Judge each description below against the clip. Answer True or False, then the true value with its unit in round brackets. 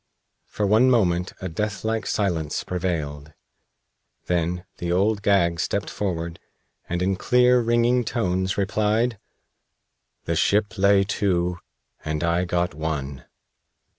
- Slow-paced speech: True (115 wpm)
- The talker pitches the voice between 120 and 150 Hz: False (95 Hz)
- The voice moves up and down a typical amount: True (3.8 semitones)